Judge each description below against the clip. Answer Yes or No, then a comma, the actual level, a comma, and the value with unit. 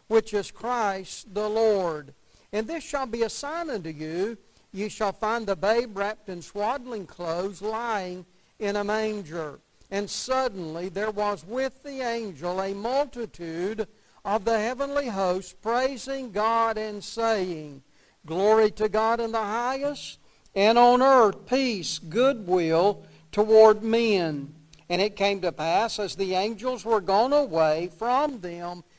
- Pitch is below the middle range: No, high, 210 Hz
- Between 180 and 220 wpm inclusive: No, average, 145 wpm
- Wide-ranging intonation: No, average, 4.1 semitones